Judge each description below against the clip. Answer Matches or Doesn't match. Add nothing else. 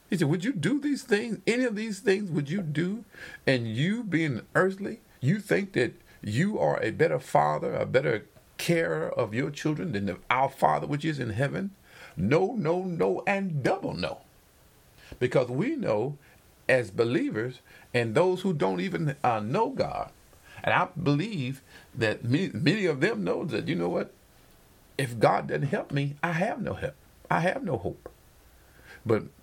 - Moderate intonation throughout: Doesn't match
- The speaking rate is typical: Matches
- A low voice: Doesn't match